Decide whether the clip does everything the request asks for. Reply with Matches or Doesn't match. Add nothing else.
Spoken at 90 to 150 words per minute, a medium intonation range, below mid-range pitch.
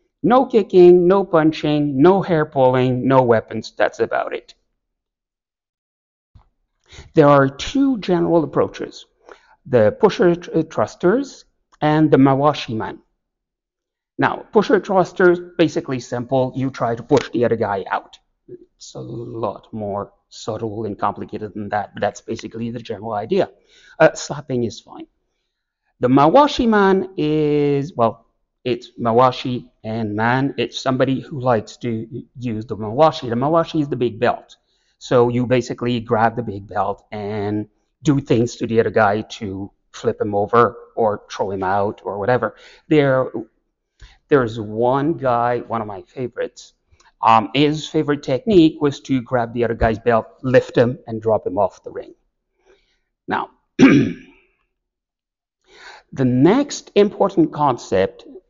Doesn't match